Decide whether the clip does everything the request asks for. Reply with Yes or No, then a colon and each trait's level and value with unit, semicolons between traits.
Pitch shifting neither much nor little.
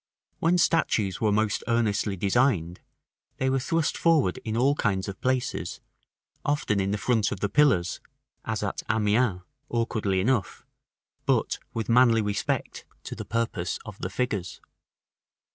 Yes: average, 4.2 semitones